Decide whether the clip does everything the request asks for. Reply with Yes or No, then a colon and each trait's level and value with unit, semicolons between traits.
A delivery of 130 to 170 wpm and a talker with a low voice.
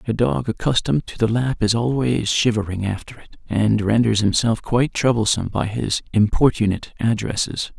Yes: average, 155 wpm; low, 110 Hz